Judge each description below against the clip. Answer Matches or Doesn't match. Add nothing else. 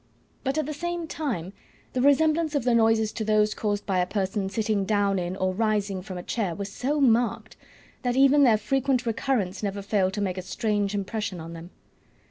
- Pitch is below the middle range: Doesn't match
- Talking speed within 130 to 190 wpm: Doesn't match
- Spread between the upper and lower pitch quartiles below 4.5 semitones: Doesn't match